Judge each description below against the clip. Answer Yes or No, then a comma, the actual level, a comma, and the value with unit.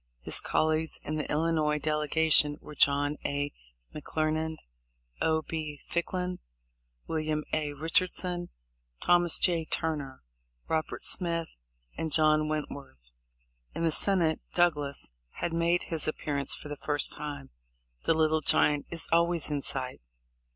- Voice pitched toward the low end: No, medium, 155 Hz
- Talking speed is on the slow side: Yes, slow, 130 wpm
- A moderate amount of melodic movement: No, narrow, 1.9 semitones